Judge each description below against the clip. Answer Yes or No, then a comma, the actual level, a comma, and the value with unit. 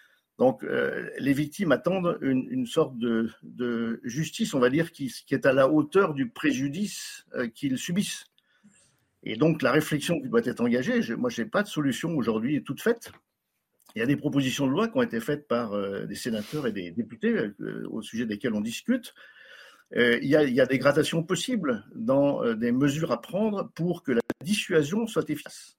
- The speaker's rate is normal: Yes, average, 205 wpm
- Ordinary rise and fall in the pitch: No, wide, 9.0 semitones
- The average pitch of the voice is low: No, medium, 170 Hz